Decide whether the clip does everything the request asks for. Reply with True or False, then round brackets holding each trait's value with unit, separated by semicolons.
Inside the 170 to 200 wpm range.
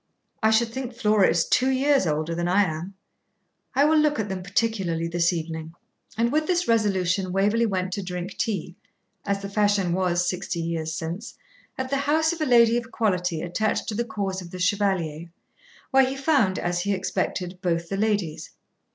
True (185 wpm)